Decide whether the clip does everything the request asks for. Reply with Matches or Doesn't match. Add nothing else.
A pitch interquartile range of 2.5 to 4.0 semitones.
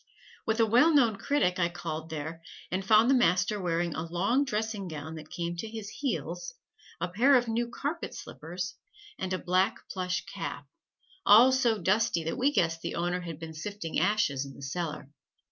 Doesn't match